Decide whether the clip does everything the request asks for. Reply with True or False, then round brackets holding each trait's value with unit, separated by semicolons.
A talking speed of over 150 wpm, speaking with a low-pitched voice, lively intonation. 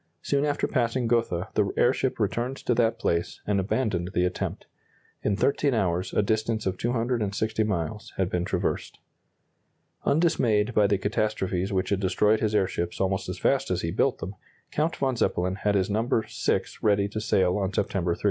False (175 wpm; 105 Hz; 3.5 semitones)